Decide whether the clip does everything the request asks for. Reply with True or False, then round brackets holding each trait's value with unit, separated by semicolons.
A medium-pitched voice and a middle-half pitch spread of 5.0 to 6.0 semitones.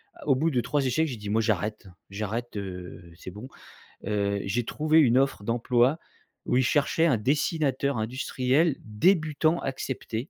False (125 Hz; 5.4 semitones)